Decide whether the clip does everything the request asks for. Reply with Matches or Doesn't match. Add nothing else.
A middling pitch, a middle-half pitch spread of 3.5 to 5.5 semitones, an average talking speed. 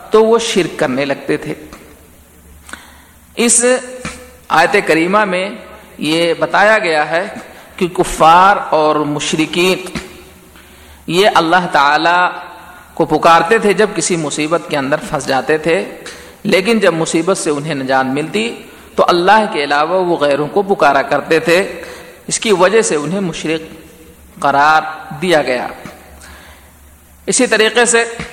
Matches